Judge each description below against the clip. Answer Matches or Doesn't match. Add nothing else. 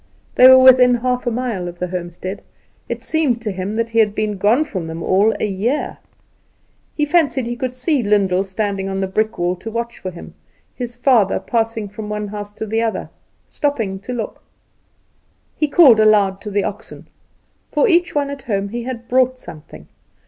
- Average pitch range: Matches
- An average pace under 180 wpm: Doesn't match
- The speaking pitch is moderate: Doesn't match